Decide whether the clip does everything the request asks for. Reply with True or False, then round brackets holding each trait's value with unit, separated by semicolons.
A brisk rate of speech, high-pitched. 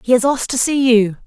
True (285 wpm; 245 Hz)